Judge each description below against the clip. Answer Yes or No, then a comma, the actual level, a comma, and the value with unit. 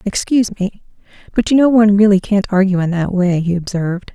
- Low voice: No, high, 195 Hz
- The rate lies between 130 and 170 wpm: No, fast, 205 wpm